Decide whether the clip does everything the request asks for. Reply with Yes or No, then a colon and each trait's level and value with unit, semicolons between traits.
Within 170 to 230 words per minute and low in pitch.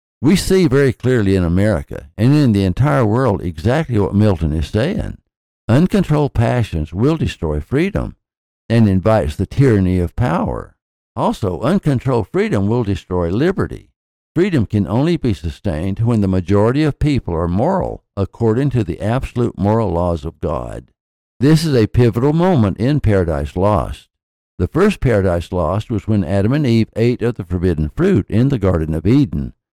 No: average, 160 wpm; low, 105 Hz